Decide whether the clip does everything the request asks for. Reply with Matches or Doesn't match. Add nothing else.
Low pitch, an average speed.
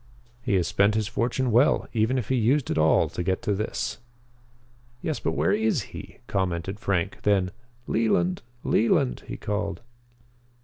Matches